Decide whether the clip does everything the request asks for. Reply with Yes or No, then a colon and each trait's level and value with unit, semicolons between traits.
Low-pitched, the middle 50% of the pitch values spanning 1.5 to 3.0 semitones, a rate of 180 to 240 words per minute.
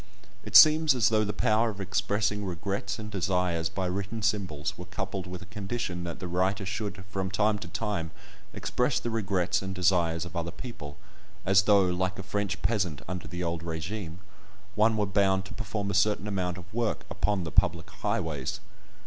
Yes: very low, 95 Hz; average, 2.7 semitones; average, 185 wpm